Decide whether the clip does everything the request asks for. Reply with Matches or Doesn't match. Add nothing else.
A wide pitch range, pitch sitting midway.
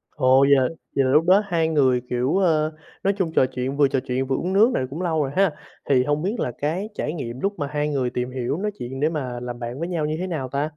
Doesn't match